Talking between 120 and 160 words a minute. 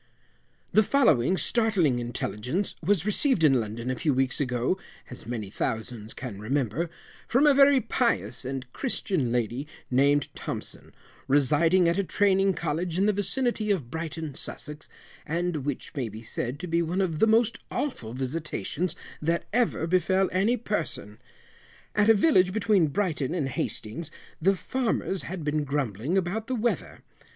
Yes: average, 155 wpm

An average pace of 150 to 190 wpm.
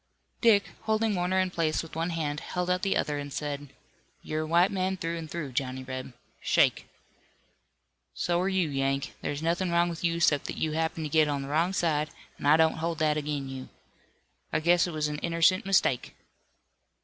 No: average, 200 wpm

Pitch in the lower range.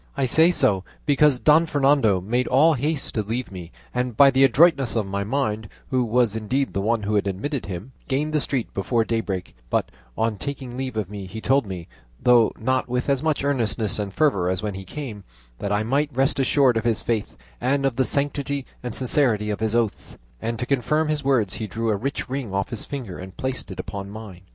Yes: low, 120 Hz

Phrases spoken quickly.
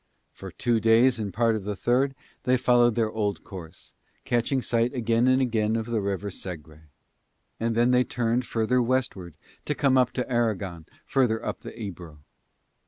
No: average, 170 wpm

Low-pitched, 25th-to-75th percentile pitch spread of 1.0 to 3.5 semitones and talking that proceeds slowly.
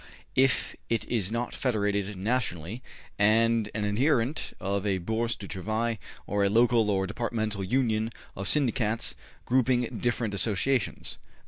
Yes: low, 110 Hz; average, 2.9 semitones; slow, 130 wpm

